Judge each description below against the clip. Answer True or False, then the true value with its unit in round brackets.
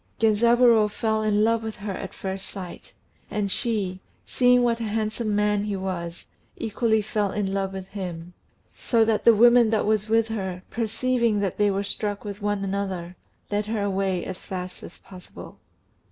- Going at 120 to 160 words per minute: False (175 wpm)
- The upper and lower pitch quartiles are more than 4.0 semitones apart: False (2.5 semitones)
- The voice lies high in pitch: True (210 Hz)